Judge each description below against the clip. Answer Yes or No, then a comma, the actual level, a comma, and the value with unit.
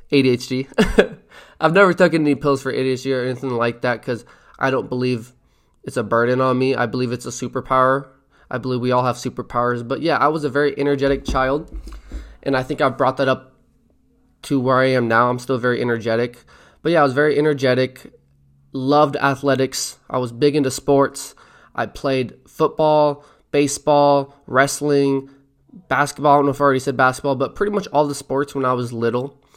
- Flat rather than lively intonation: Yes, narrow, 2.1 semitones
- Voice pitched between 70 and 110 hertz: No, low, 135 Hz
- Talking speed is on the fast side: No, average, 190 wpm